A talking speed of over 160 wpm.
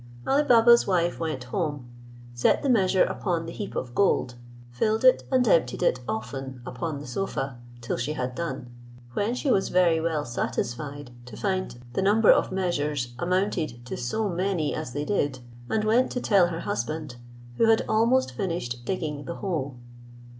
Yes: average, 170 wpm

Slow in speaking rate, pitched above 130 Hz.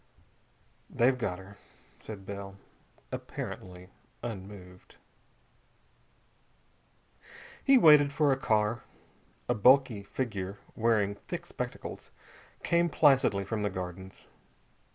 No: slow, 90 wpm; low, 105 Hz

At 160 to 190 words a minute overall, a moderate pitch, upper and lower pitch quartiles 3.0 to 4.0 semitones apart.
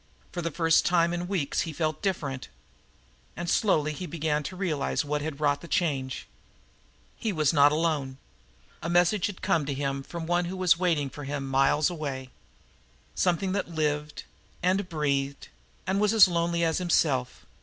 Yes: average, 175 wpm; medium, 160 Hz; average, 3.4 semitones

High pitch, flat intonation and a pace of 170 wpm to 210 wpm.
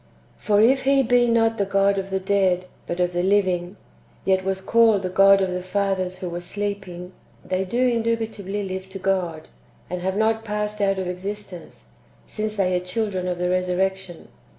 Yes: high, 195 Hz; narrow, 2.3 semitones; average, 185 wpm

